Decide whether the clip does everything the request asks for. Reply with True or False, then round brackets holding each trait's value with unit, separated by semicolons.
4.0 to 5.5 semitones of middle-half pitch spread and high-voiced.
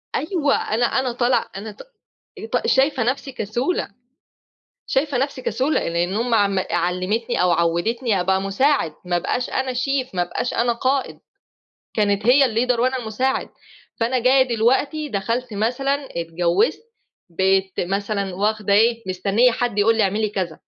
True (4.8 semitones; 230 Hz)